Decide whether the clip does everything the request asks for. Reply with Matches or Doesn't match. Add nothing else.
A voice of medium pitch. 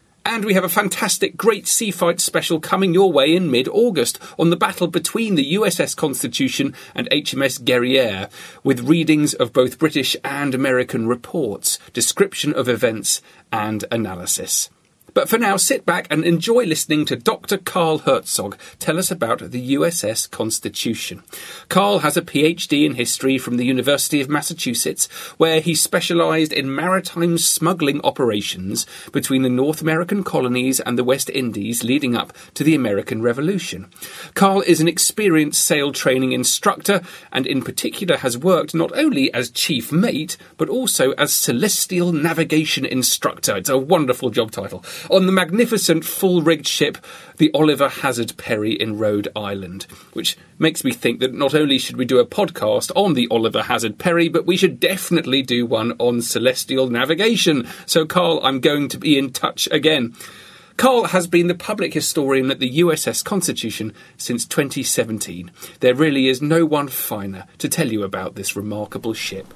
Matches